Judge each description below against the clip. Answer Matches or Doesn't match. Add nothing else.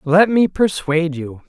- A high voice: Doesn't match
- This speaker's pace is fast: Doesn't match